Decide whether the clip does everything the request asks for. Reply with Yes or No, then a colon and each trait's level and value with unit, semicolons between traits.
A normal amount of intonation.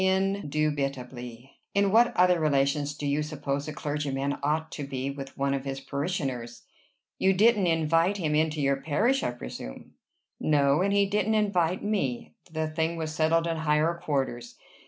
Yes: average, 4.2 semitones